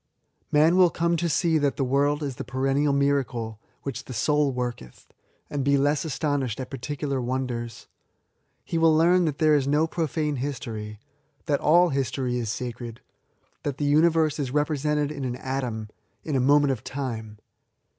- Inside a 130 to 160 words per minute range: No, average, 170 wpm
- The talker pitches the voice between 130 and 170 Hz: Yes, medium, 140 Hz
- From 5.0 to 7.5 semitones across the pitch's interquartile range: No, average, 3.0 semitones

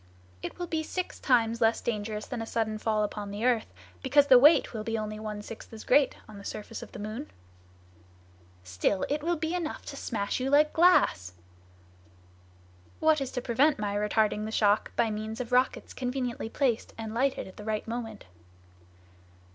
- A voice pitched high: Yes, high, 225 Hz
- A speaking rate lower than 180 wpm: No, average, 185 wpm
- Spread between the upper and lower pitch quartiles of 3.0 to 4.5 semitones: Yes, average, 4.2 semitones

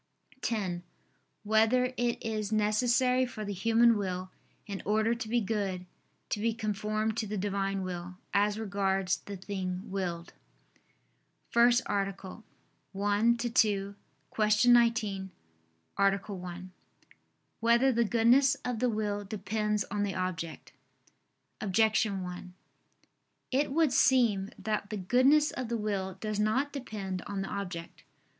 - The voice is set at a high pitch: Yes, high, 210 Hz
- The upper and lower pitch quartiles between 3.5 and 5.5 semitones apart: No, average, 3.0 semitones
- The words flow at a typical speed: No, slow, 130 wpm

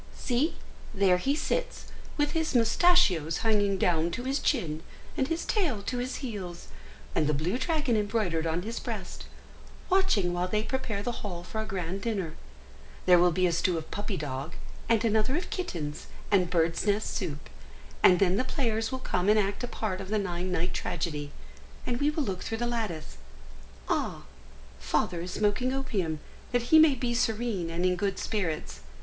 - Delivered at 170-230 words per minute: Yes, average, 180 wpm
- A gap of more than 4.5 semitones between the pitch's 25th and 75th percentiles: Yes, wide, 5.6 semitones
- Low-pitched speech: No, high, 205 Hz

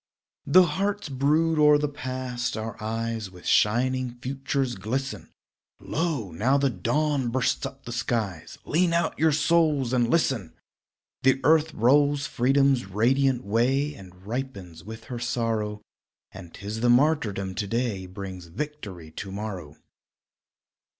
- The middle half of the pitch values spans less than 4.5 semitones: No, average, 5.1 semitones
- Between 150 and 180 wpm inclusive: No, slow, 135 wpm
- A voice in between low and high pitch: No, low, 125 Hz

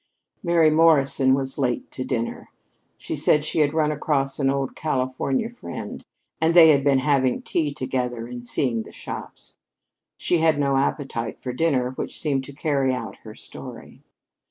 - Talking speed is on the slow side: No, average, 165 wpm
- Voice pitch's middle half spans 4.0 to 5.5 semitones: No, average, 2.9 semitones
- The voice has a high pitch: No, low, 135 Hz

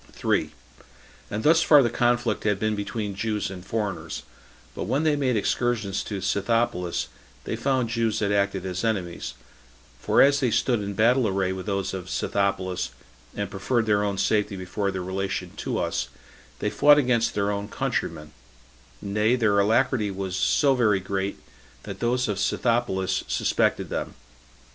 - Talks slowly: No, average, 160 wpm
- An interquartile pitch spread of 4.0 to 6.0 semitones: No, average, 3.5 semitones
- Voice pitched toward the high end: No, low, 105 Hz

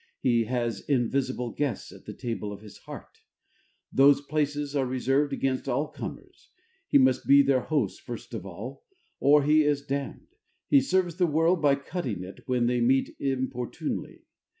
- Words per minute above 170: No, average, 165 wpm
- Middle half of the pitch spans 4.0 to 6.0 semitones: No, average, 3.1 semitones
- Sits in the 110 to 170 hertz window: Yes, low, 135 Hz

